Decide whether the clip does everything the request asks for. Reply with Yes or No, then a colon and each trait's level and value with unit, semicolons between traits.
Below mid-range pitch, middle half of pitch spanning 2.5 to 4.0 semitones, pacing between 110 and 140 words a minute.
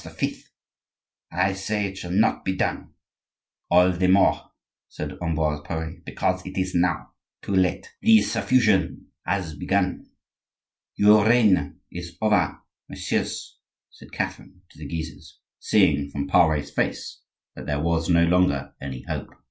Yes: very low, 90 Hz; average, 3.3 semitones; slow, 135 wpm